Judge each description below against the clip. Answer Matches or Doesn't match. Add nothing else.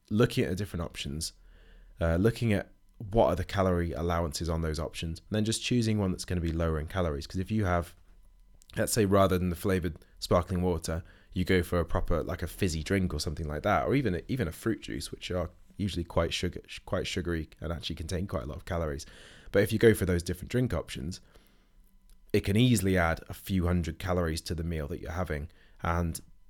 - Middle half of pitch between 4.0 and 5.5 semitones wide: Doesn't match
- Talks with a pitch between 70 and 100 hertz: Matches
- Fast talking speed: Matches